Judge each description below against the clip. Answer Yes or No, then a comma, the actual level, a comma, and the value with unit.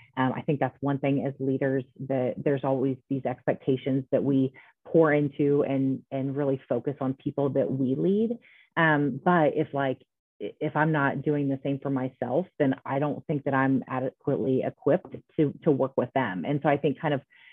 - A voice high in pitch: No, medium, 140 Hz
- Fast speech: No, average, 195 wpm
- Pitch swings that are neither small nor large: No, narrow, 1.7 semitones